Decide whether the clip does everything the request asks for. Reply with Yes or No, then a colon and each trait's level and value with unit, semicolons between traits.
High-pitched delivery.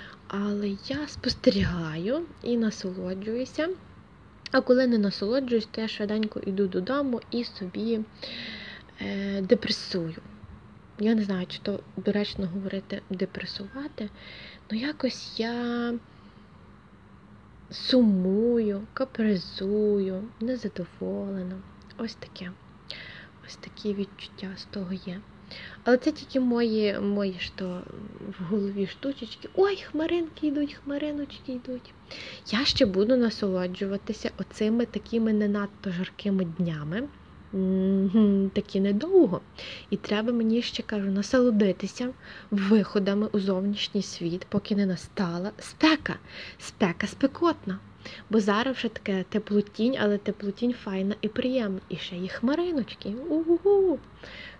Yes: high, 210 Hz